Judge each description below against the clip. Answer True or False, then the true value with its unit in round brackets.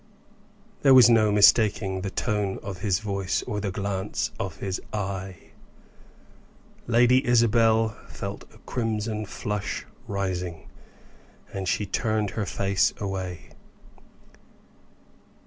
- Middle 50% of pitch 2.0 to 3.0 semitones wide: True (2.5 semitones)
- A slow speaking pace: True (110 wpm)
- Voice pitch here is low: True (105 Hz)